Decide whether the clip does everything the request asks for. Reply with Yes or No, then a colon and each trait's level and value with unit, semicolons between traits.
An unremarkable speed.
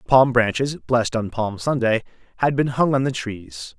Yes: average, 190 wpm